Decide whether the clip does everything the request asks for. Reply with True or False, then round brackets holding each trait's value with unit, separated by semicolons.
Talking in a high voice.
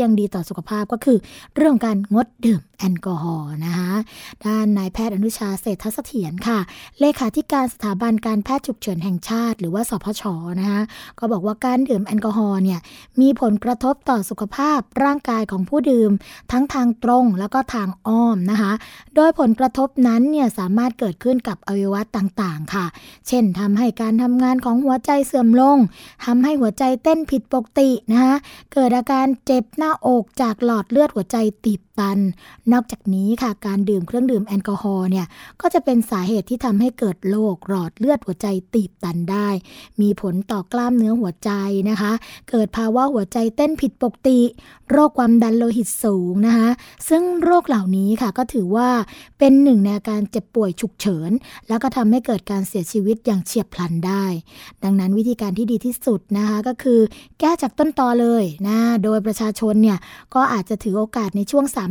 True (225 Hz)